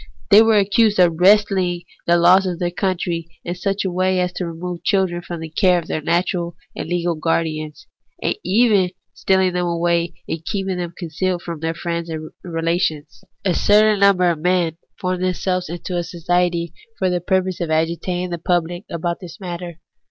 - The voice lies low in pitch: No, medium, 175 Hz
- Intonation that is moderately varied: No, narrow, 1.7 semitones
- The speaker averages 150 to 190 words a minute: Yes, average, 185 wpm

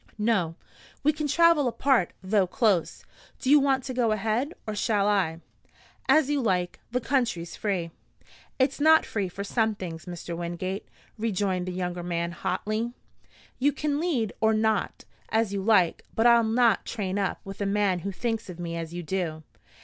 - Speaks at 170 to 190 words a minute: Yes, average, 175 wpm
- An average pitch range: Yes, average, 5.0 semitones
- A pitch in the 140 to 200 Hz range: No, high, 210 Hz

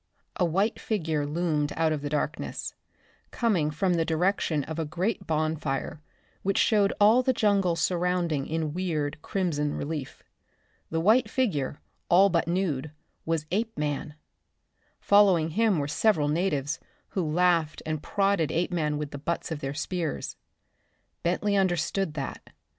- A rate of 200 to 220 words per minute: No, average, 140 wpm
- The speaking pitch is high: No, medium, 165 Hz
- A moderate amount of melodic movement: Yes, average, 4.1 semitones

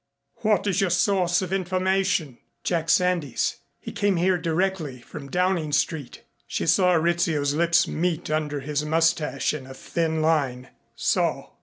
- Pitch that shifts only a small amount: No, average, 3.3 semitones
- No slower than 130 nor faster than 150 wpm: Yes, average, 145 wpm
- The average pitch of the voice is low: No, medium, 165 Hz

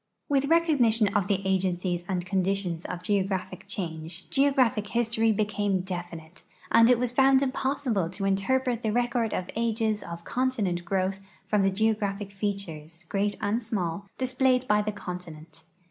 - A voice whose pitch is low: No, high, 205 Hz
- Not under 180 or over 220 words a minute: No, average, 145 wpm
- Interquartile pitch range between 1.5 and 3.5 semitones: No, average, 4.2 semitones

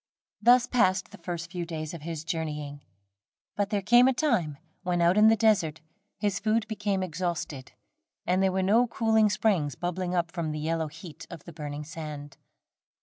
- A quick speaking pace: No, average, 180 wpm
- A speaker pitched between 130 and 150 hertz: No, medium, 175 Hz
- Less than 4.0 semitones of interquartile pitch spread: No, average, 4.6 semitones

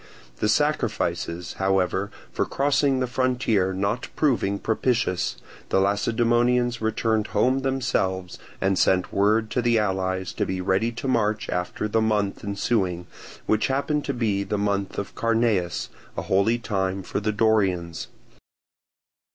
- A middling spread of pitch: Yes, average, 3.7 semitones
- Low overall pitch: Yes, low, 105 Hz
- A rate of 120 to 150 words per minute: Yes, slow, 135 wpm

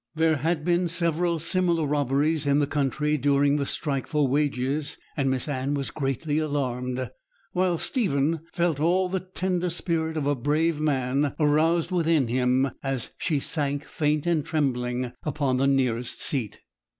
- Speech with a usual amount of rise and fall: Yes, average, 3.2 semitones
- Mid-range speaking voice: Yes, medium, 150 Hz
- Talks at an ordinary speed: Yes, average, 155 wpm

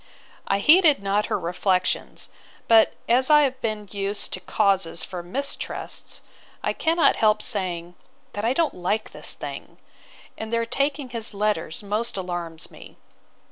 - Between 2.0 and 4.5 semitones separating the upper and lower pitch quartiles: No, average, 4.9 semitones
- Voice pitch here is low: No, high, 210 Hz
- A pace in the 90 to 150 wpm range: Yes, average, 145 wpm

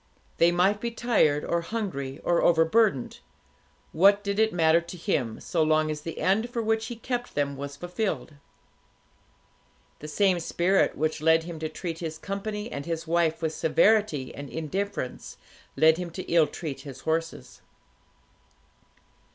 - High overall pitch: No, medium, 170 Hz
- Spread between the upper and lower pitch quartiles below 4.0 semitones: No, average, 4.3 semitones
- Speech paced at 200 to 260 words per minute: No, average, 155 wpm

